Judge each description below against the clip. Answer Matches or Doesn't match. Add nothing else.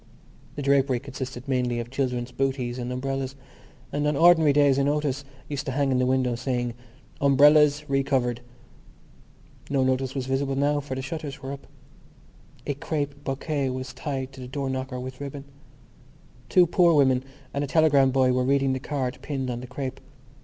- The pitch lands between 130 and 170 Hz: Matches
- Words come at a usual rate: Matches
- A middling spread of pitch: Doesn't match